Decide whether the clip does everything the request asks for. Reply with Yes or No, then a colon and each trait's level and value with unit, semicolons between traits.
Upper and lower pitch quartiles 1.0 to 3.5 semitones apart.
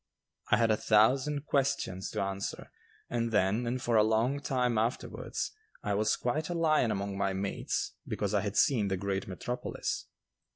No: average, 4.2 semitones